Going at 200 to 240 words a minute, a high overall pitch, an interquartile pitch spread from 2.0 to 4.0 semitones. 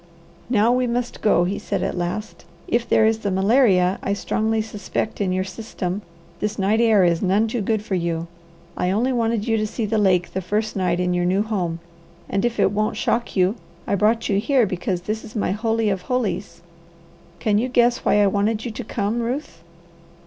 Yes: fast, 205 wpm; high, 210 Hz; average, 3.1 semitones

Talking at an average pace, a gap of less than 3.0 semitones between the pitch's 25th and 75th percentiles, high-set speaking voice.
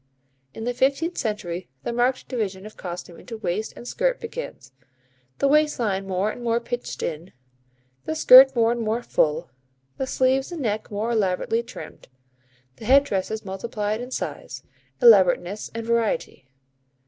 No: average, 155 wpm; average, 4.4 semitones; high, 230 Hz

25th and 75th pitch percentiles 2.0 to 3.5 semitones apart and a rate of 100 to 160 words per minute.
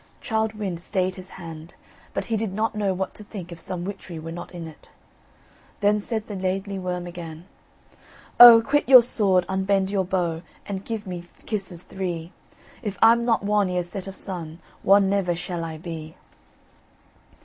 No: average, 3.0 semitones; average, 175 wpm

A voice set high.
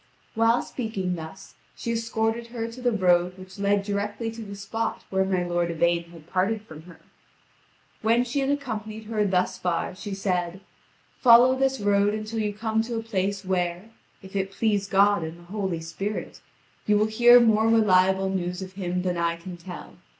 Yes: high, 200 Hz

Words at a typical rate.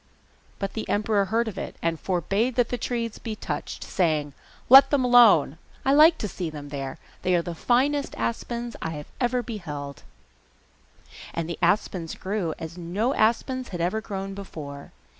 Yes: average, 170 wpm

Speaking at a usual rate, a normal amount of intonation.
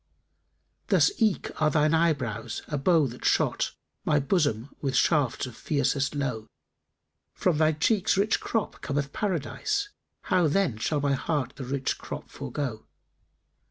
Yes: average, 150 wpm; average, 4.0 semitones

